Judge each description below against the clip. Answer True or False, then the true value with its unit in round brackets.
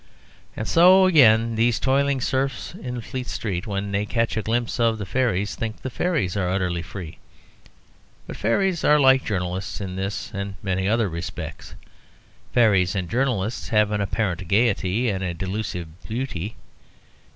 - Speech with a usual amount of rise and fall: True (4.6 semitones)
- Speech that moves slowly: False (155 wpm)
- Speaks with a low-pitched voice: True (110 Hz)